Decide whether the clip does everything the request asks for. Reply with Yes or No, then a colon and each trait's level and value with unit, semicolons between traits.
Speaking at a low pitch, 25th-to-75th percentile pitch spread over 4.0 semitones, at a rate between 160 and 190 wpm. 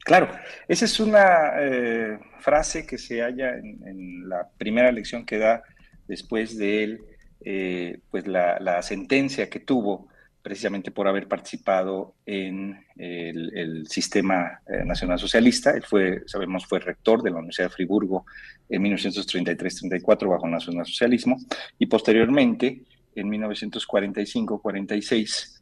No: low, 105 Hz; average, 4.7 semitones; average, 130 wpm